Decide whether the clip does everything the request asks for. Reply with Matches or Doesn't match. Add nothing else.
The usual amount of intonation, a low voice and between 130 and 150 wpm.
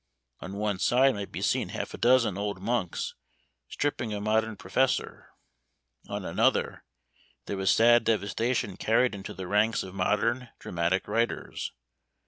Matches